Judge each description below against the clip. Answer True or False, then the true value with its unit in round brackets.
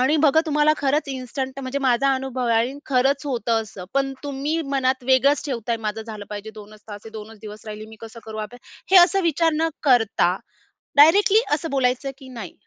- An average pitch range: True (4.0 semitones)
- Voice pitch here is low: False (260 Hz)